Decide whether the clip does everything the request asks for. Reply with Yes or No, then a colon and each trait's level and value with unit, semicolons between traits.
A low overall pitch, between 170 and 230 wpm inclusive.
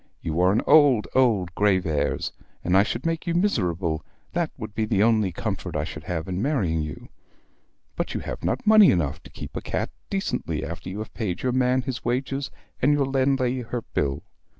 Yes: low, 110 Hz; average, 195 wpm